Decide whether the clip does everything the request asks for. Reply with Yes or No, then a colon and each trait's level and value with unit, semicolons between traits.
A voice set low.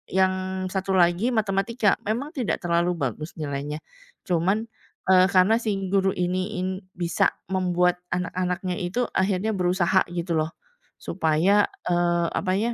No: medium, 185 Hz